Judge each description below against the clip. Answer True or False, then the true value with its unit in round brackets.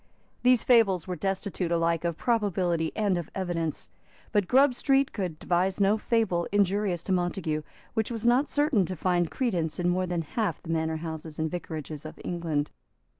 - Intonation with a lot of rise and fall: False (4.1 semitones)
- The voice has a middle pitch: True (180 Hz)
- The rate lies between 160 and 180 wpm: True (175 wpm)